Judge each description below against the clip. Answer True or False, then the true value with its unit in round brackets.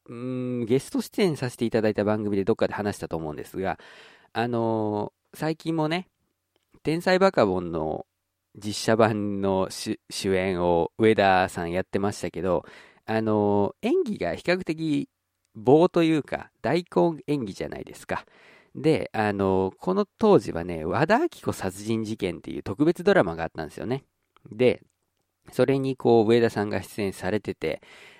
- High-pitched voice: False (110 Hz)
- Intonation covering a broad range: True (8.1 semitones)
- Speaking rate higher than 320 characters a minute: False (305 characters per minute)